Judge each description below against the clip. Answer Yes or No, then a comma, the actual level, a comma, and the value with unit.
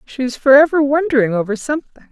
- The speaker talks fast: No, average, 170 wpm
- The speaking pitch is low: No, very high, 265 Hz